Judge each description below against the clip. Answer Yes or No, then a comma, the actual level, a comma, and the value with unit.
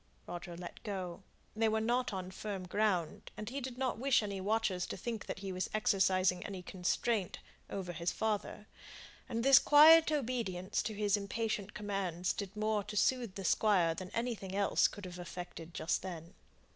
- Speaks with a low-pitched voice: No, high, 200 Hz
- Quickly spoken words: No, average, 175 wpm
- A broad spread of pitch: No, average, 3.3 semitones